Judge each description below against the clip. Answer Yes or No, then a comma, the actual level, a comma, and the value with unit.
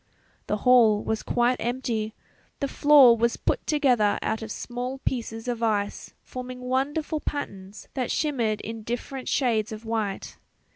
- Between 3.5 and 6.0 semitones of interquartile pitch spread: No, average, 2.9 semitones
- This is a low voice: No, high, 240 Hz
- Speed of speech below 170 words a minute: Yes, average, 145 wpm